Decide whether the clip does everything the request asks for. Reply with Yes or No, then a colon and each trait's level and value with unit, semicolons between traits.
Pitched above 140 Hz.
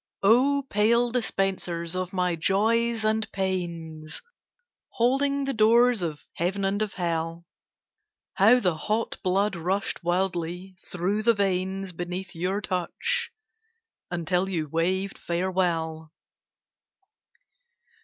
Yes: high, 190 Hz